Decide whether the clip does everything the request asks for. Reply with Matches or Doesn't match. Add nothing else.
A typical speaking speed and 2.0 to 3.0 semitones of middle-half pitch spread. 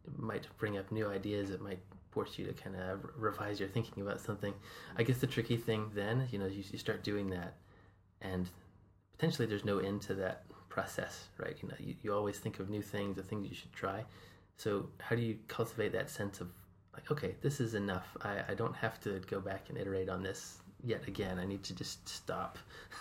Doesn't match